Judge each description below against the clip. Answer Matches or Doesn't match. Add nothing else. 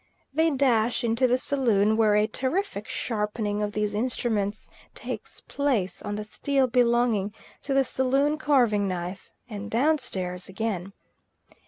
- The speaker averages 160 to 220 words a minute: Doesn't match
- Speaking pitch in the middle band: Doesn't match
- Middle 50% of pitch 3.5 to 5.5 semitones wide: Matches